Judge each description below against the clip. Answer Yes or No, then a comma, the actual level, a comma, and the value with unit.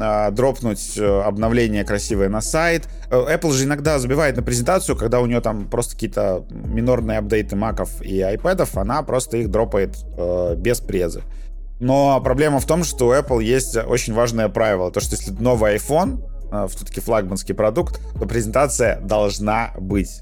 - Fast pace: No, average, 150 wpm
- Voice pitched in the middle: No, low, 110 Hz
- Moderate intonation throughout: Yes, average, 3.4 semitones